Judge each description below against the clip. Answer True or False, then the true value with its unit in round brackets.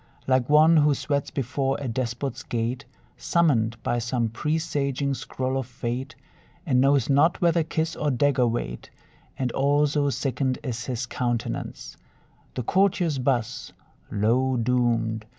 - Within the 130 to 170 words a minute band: True (135 wpm)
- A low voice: True (130 Hz)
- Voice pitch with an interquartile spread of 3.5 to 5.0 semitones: False (3.1 semitones)